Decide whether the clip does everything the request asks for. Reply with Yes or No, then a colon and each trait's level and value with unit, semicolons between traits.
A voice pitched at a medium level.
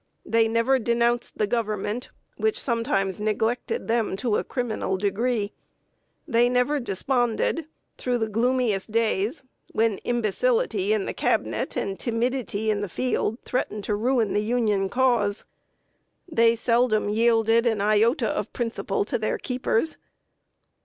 No: high, 230 Hz